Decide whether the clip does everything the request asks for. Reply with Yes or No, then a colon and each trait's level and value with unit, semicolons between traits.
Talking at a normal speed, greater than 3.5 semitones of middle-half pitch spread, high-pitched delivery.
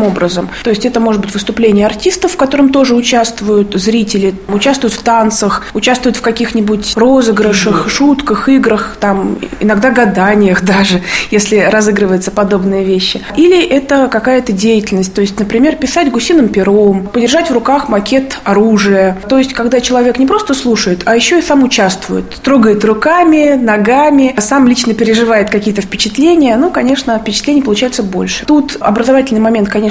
Yes: average, 150 wpm; average, 4.2 semitones; high, 225 Hz